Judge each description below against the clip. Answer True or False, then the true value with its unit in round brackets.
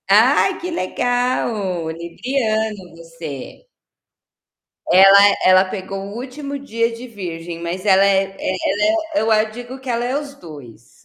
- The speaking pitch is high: True (210 Hz)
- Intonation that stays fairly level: False (5.6 semitones)